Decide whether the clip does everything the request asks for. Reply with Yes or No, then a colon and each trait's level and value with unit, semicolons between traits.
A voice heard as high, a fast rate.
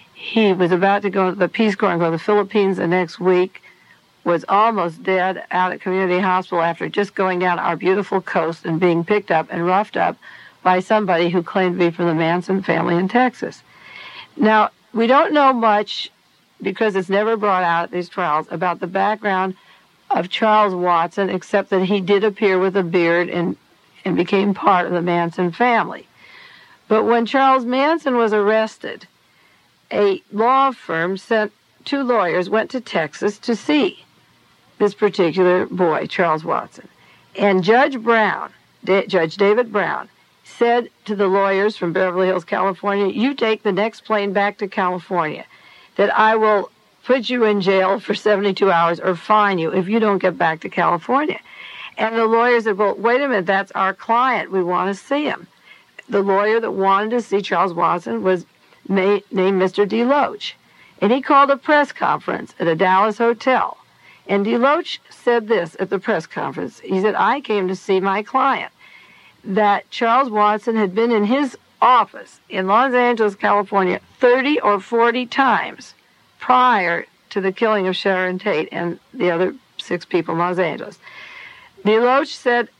No: high, 200 Hz; average, 170 wpm